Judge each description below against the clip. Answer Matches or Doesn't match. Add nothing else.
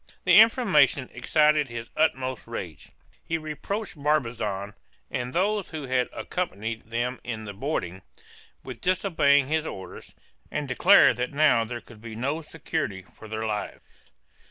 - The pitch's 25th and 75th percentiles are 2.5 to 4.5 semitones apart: Doesn't match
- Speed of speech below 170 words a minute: Matches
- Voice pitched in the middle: Doesn't match